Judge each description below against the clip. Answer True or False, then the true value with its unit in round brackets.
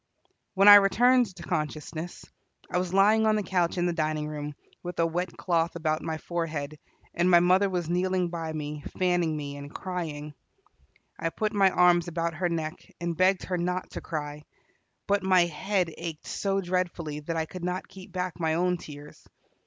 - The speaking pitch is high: False (175 Hz)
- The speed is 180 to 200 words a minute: True (185 wpm)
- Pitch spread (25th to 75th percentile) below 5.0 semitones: True (2.6 semitones)